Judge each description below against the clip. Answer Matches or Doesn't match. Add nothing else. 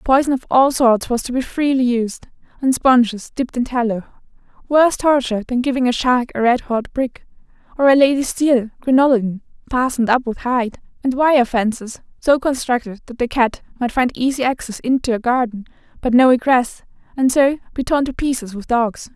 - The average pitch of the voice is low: Doesn't match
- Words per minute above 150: Matches